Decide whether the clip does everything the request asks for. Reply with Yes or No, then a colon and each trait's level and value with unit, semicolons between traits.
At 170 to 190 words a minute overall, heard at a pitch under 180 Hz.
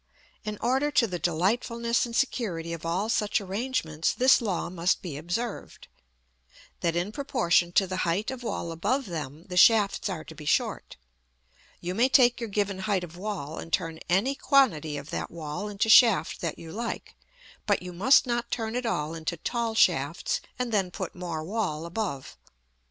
No: average, 180 wpm; high, 195 Hz